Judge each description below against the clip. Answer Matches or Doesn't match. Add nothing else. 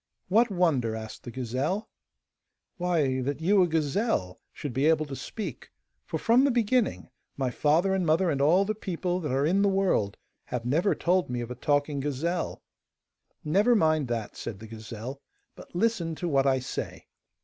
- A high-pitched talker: Doesn't match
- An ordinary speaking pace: Matches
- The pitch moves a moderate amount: Doesn't match